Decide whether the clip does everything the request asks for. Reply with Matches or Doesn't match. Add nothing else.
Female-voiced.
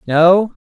Matches